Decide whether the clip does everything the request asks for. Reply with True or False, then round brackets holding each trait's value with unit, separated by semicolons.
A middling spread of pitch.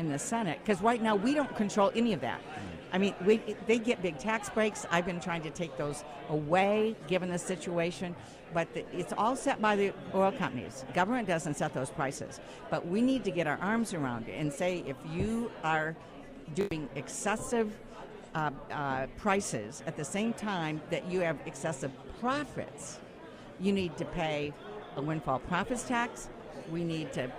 False (5.7 semitones)